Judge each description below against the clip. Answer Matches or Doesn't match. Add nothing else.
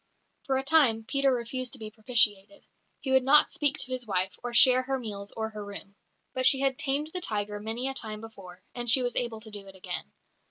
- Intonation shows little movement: Doesn't match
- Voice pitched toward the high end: Matches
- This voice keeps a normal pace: Doesn't match